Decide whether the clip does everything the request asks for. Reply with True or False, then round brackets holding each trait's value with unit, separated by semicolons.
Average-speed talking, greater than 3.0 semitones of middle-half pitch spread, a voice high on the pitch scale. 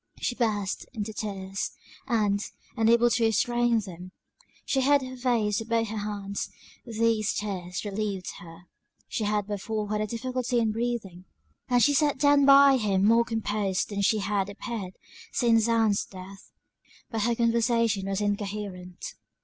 False (150 wpm; 2.7 semitones; 215 Hz)